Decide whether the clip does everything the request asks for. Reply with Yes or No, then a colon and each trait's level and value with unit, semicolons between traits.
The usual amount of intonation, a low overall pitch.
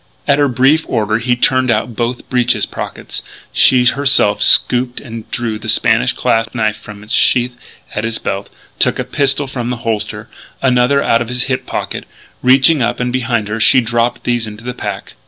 No: narrow, 2.2 semitones; low, 120 Hz